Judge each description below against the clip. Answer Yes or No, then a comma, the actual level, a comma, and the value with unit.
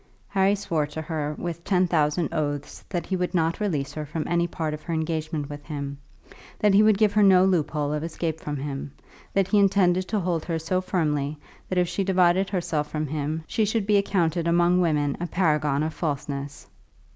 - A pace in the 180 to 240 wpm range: Yes, fast, 205 wpm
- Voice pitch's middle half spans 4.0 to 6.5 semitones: No, average, 3.6 semitones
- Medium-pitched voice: Yes, medium, 165 Hz